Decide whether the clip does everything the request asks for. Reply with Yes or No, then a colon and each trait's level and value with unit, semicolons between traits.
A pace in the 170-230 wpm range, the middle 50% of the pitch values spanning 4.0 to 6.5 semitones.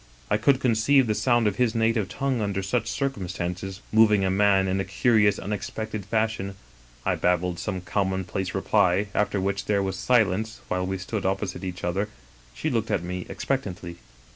No: average, 180 wpm; average, 2.9 semitones